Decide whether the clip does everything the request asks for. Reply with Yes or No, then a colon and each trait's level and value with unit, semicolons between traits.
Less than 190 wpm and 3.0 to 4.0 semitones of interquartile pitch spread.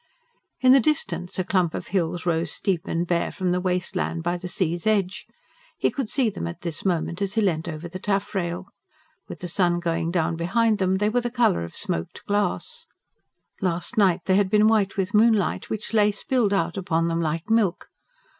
No: average, 200 wpm; average, 3.5 semitones